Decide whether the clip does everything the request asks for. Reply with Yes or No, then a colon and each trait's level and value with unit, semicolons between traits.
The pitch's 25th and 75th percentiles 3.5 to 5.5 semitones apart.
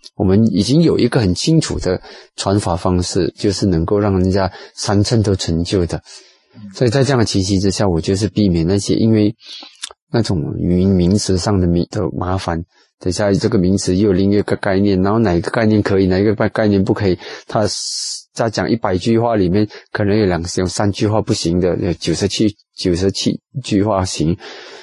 No: narrow, 2.6 semitones